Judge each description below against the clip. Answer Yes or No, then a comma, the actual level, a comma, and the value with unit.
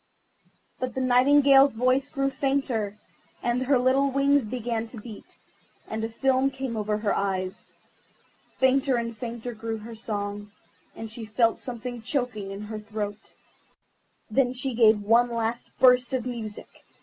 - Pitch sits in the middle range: No, high, 235 Hz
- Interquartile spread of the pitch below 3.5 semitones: Yes, average, 3.1 semitones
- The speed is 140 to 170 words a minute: Yes, average, 150 wpm